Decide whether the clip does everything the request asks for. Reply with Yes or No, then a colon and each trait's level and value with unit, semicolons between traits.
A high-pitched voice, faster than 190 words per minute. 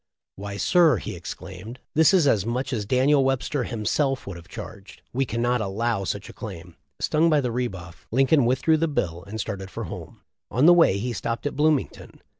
No: low, 120 Hz; average, 200 wpm